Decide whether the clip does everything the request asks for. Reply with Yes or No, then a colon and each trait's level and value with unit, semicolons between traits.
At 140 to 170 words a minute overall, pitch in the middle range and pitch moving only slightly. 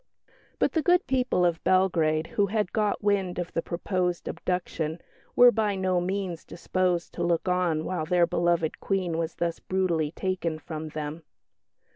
Yes: average, 160 wpm; medium, 180 Hz; narrow, 2.3 semitones